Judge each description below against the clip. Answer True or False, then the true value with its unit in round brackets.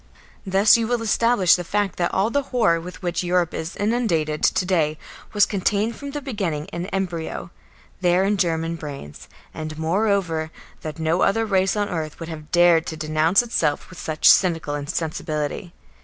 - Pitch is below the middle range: False (175 Hz)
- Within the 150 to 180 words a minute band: True (170 wpm)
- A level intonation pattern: False (4.1 semitones)